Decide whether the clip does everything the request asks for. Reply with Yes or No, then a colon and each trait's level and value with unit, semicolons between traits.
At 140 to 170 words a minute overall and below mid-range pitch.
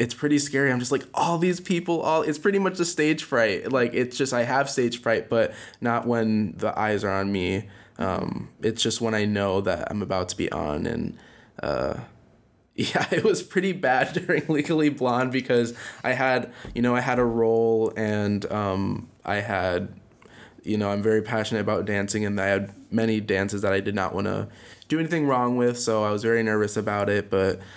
No: fast, 205 wpm; low, 115 Hz